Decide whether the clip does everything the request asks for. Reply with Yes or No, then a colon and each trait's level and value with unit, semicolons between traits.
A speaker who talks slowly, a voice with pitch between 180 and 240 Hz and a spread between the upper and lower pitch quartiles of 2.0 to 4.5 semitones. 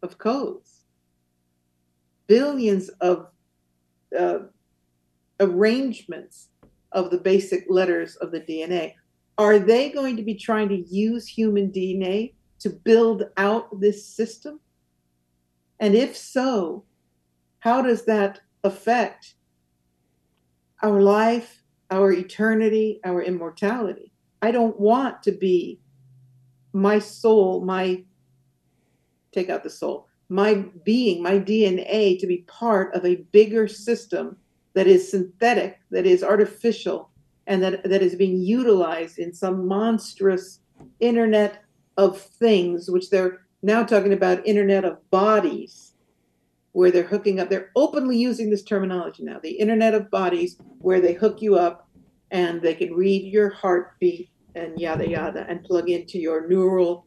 Yes: slow, 130 wpm; high, 190 Hz; average, 3.6 semitones